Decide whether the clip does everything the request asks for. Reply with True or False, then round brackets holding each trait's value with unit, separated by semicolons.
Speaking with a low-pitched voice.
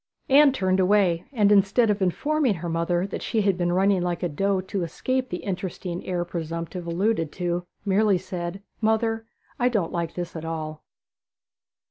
False (185 Hz)